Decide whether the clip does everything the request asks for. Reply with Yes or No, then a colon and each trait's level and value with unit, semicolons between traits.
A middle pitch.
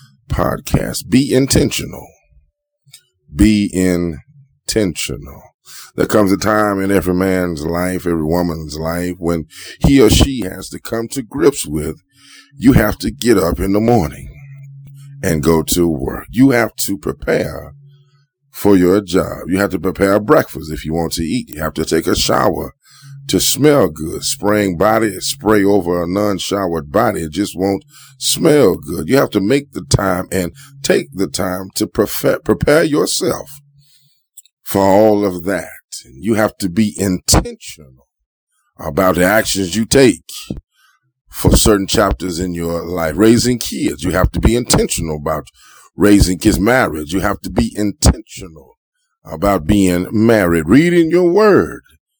No: low, 100 Hz